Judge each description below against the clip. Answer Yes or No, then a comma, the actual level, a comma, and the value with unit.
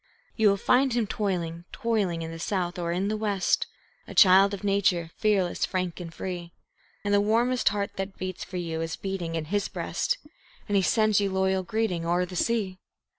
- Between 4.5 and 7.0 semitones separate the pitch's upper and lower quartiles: No, average, 2.9 semitones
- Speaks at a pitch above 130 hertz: Yes, high, 190 Hz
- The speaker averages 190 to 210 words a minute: Yes, average, 195 wpm